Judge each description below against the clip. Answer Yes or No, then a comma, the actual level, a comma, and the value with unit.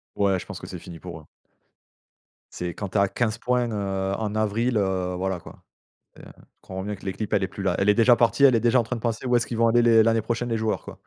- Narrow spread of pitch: No, average, 3.4 semitones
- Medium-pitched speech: No, low, 110 Hz